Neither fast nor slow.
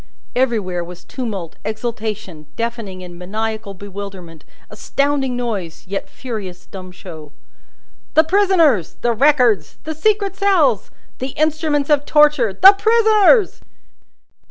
No: slow, 110 wpm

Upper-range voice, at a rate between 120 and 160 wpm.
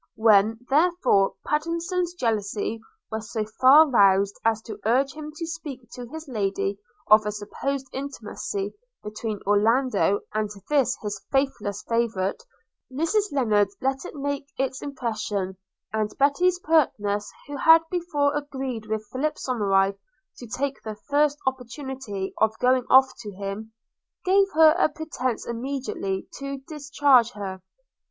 Yes: very high, 250 Hz; slow, 135 wpm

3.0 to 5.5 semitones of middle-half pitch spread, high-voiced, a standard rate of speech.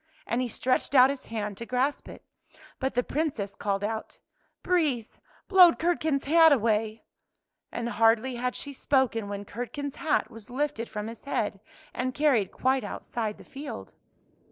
Yes: average, 4.3 semitones; very high, 250 Hz; average, 170 wpm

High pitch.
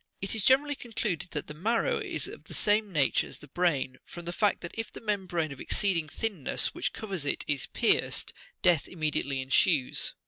No: medium, 175 Hz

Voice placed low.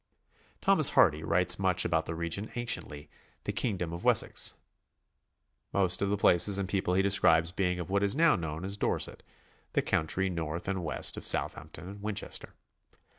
Yes: very low, 90 Hz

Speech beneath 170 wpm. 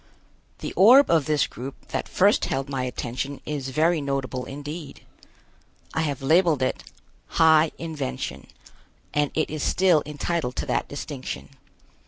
Yes: average, 140 wpm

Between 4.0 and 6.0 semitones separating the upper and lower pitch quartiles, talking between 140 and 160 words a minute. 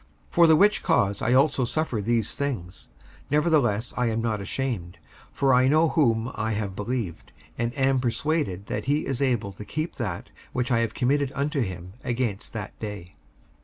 No: average, 5.0 semitones; average, 180 wpm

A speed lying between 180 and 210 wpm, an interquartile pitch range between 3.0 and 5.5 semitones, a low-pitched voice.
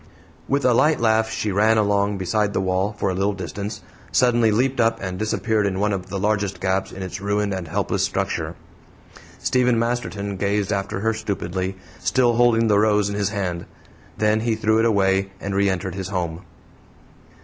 No: average, 185 wpm; narrow, 2.5 semitones; low, 100 Hz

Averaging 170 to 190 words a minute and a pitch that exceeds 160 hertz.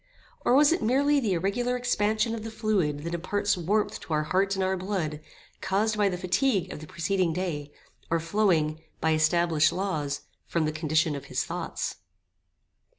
Yes: average, 175 wpm; medium, 185 Hz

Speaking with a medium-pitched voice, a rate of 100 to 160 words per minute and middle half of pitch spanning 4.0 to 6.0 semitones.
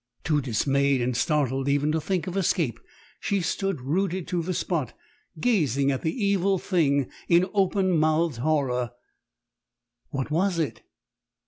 Yes: medium, 155 Hz; average, 140 wpm; average, 5.0 semitones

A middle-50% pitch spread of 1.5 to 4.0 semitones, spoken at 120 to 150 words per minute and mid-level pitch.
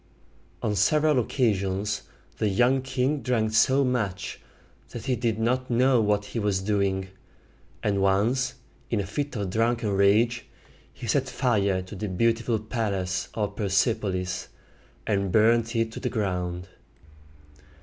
No: average, 3.5 semitones; average, 145 wpm; low, 110 Hz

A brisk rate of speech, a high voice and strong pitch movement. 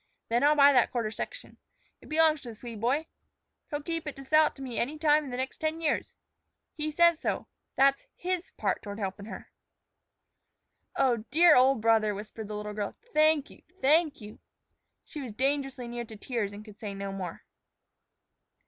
No: average, 190 wpm; very high, 265 Hz; wide, 5.9 semitones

